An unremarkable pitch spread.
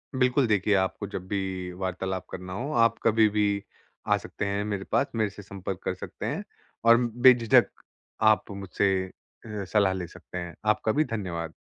Yes: average, 3.0 semitones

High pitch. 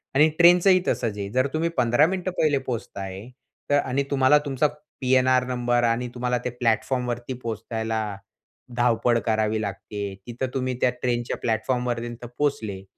No: low, 125 Hz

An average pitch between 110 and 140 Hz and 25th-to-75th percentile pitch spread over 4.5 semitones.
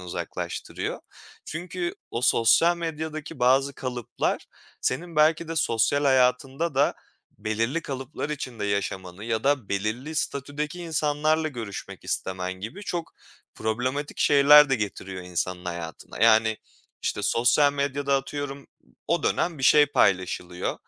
Yes: low, 135 Hz; wide, 5.5 semitones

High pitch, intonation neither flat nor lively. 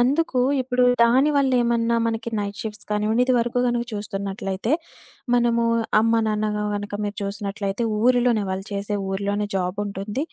Yes: high, 215 Hz; average, 3.0 semitones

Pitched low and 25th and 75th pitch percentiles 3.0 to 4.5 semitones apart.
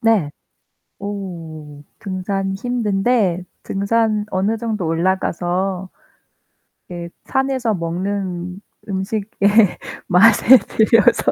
No: high, 195 Hz; average, 3.6 semitones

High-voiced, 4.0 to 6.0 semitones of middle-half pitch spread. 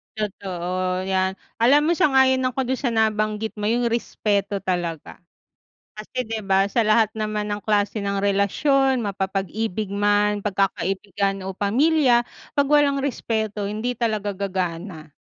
No: high, 210 Hz; average, 3.2 semitones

